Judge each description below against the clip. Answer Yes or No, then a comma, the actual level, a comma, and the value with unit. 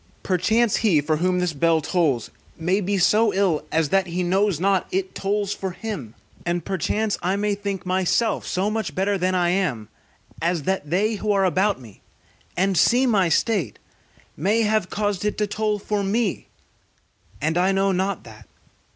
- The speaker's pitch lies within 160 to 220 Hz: Yes, high, 190 Hz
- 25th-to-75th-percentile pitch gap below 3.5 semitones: Yes, average, 3.0 semitones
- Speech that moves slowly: No, average, 175 wpm